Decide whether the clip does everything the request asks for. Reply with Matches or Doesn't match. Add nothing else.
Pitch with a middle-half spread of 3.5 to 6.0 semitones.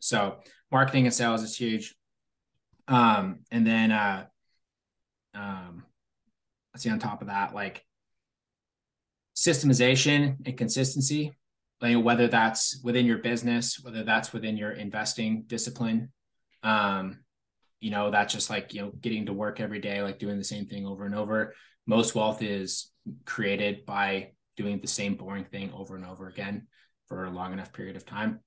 Doesn't match